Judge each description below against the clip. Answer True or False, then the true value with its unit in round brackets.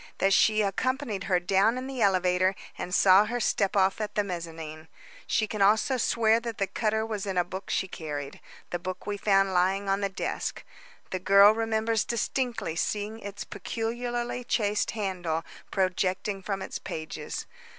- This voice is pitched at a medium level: False (200 Hz)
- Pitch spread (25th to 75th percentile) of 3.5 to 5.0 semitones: False (3.0 semitones)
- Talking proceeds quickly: False (170 wpm)